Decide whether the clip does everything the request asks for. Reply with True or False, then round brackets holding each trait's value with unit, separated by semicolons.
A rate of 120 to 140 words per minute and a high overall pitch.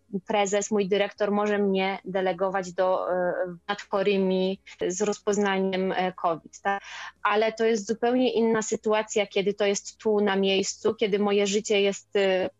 True (130 wpm; 200 Hz)